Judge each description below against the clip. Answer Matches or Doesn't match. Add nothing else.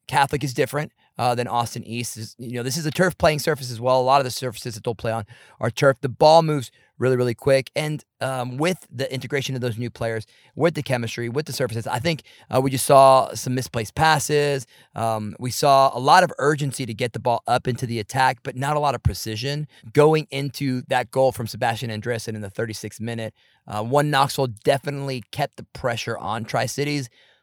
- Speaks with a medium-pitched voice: Doesn't match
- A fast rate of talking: Matches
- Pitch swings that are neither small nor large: Matches